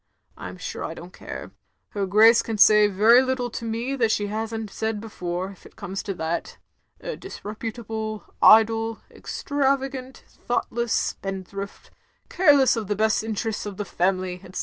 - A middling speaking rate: Yes, average, 165 wpm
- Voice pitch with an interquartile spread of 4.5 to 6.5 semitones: No, average, 2.9 semitones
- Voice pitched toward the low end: No, high, 220 Hz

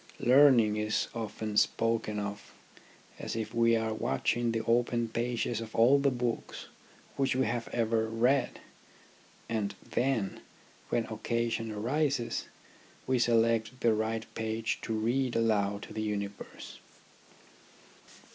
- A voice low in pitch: Yes, low, 115 Hz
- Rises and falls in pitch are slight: Yes, narrow, 1.6 semitones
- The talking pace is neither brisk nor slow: No, slow, 125 wpm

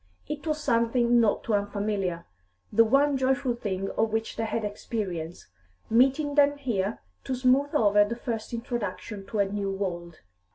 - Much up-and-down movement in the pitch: No, average, 4.2 semitones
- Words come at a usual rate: Yes, average, 160 wpm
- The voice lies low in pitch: No, high, 225 Hz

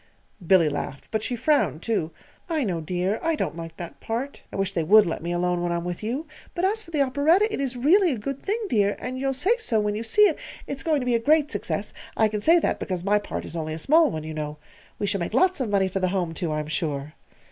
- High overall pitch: Yes, high, 210 Hz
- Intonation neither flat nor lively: No, wide, 8.5 semitones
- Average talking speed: No, fast, 265 wpm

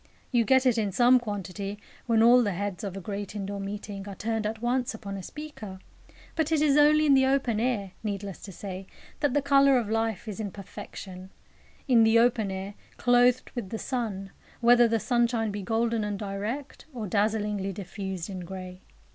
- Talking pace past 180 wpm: Yes, average, 190 wpm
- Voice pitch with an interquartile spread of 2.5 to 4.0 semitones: Yes, average, 3.6 semitones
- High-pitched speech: Yes, high, 220 Hz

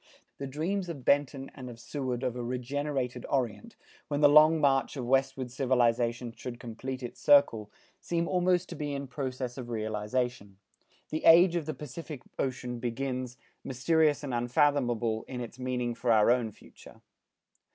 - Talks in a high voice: No, low, 130 Hz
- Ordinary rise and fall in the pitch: Yes, average, 3.1 semitones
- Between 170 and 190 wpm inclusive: No, average, 160 wpm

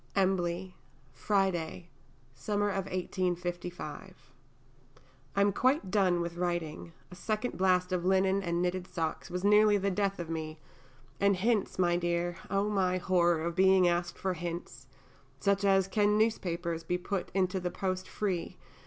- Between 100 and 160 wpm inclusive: Yes, average, 155 wpm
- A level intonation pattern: Yes, narrow, 2.1 semitones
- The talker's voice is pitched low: No, medium, 185 Hz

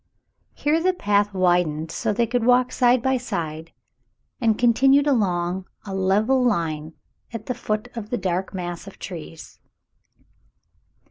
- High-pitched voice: Yes, high, 205 Hz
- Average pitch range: No, wide, 5.8 semitones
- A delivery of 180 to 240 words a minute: No, average, 145 wpm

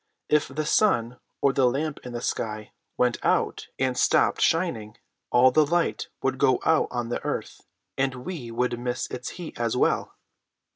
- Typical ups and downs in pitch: Yes, average, 3.8 semitones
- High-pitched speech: No, low, 125 Hz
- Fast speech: No, average, 175 wpm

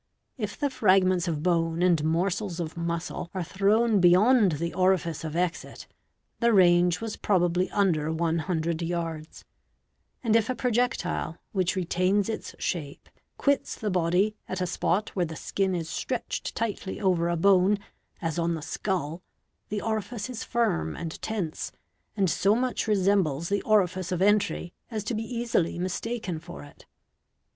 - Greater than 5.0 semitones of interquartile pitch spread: No, average, 3.7 semitones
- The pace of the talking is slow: No, average, 155 wpm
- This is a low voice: No, medium, 185 Hz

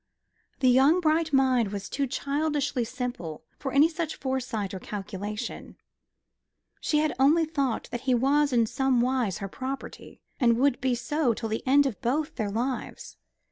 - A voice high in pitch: Yes, very high, 260 Hz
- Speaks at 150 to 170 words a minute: Yes, average, 160 wpm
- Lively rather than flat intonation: No, average, 3.6 semitones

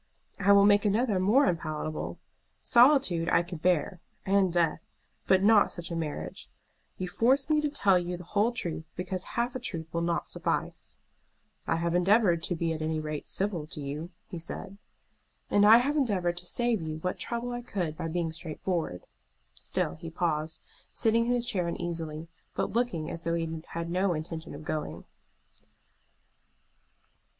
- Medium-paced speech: Yes, average, 170 wpm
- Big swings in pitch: No, average, 4.1 semitones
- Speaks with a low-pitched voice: No, medium, 175 Hz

